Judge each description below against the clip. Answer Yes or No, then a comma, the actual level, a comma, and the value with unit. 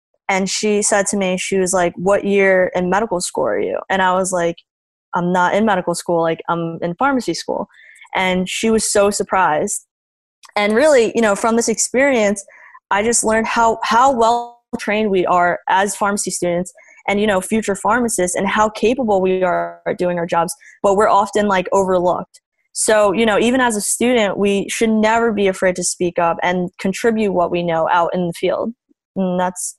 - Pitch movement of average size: Yes, average, 3.3 semitones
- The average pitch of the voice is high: Yes, high, 195 Hz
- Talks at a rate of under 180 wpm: No, average, 195 wpm